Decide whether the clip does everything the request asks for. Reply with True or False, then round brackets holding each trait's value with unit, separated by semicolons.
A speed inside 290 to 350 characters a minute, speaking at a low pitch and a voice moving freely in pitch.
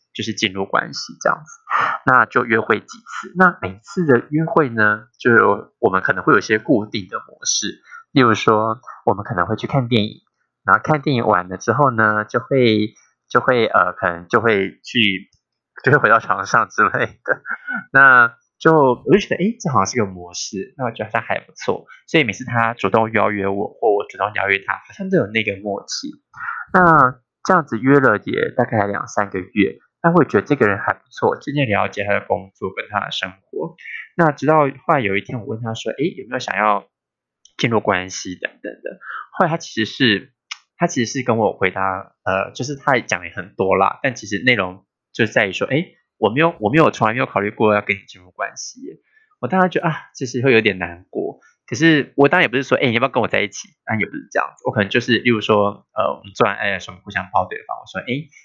True (310 characters per minute; 115 Hz; 6.0 semitones)